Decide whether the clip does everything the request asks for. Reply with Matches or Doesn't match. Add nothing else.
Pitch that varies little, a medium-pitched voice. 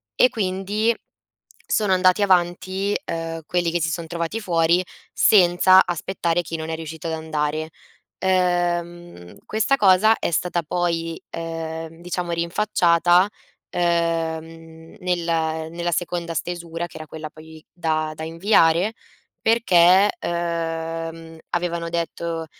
Matches